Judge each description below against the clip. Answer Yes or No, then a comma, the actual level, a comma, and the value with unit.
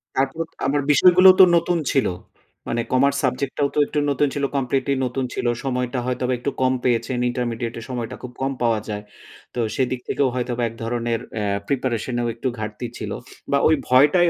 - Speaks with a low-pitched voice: Yes, low, 130 Hz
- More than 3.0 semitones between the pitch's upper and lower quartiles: No, narrow, 2.6 semitones